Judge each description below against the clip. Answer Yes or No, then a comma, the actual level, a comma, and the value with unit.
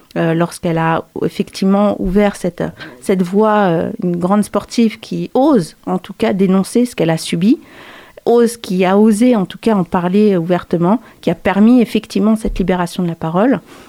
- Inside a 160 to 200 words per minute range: Yes, average, 175 wpm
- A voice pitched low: No, high, 200 Hz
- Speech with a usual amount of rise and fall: Yes, average, 3.6 semitones